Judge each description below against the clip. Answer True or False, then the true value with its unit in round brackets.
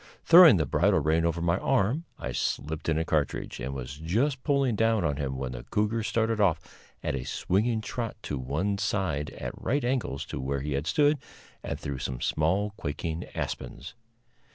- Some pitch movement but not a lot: False (8.0 semitones)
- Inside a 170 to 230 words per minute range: True (185 wpm)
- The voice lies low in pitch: True (85 Hz)